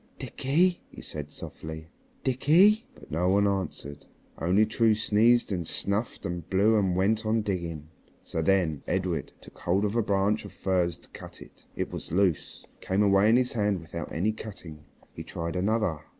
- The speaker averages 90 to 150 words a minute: No, average, 180 wpm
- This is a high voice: No, very low, 95 Hz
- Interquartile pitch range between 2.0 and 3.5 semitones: No, average, 4.2 semitones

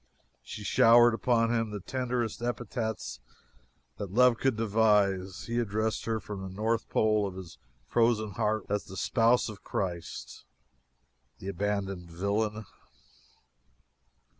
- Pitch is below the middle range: Yes, low, 110 Hz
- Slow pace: Yes, slow, 125 wpm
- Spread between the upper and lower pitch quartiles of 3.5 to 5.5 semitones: No, average, 2.7 semitones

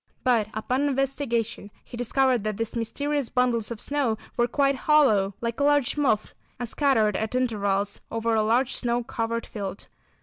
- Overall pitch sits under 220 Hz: No, high, 235 Hz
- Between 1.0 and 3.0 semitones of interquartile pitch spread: No, average, 3.5 semitones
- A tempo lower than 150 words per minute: No, average, 165 wpm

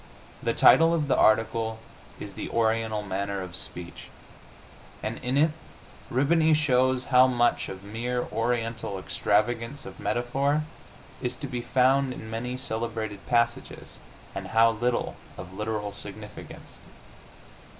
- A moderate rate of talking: No, slow, 130 wpm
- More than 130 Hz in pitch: No, low, 115 Hz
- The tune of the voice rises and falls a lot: No, average, 3.1 semitones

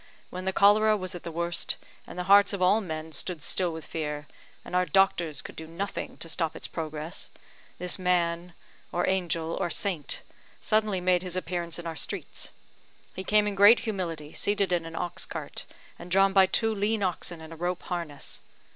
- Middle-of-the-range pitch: Yes, medium, 180 Hz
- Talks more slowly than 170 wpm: No, average, 190 wpm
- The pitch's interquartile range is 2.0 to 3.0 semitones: Yes, average, 2.7 semitones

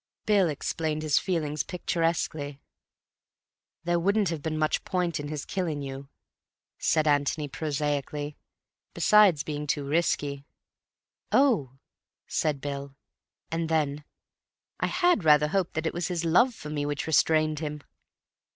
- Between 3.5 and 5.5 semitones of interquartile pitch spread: No, average, 2.8 semitones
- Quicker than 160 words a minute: No, slow, 135 wpm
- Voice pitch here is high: No, medium, 155 Hz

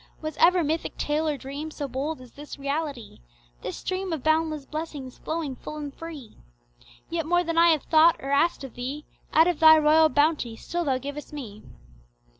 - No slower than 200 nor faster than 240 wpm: No, average, 190 wpm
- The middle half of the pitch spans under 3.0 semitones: Yes, narrow, 2.6 semitones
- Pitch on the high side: Yes, very high, 305 Hz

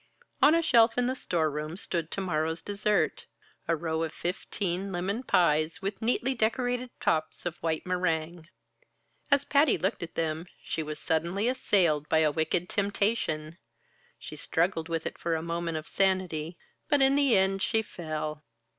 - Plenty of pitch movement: No, average, 4.7 semitones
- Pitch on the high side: No, medium, 175 Hz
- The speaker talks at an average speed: Yes, average, 165 wpm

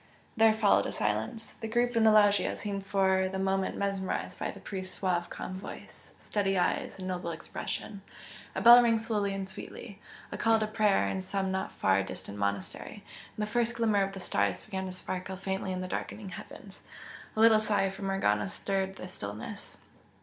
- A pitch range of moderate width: No, narrow, 2.3 semitones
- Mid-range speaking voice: No, high, 195 Hz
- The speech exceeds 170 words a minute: Yes, average, 190 wpm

